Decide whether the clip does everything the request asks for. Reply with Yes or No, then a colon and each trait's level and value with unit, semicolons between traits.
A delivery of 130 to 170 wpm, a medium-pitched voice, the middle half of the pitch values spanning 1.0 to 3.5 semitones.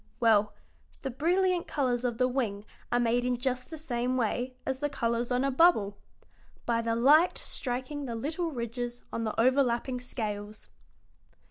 No: average, 160 wpm; high, 245 Hz; average, 2.7 semitones